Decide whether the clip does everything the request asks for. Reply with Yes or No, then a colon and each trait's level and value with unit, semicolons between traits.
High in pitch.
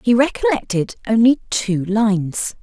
Yes: high, 225 Hz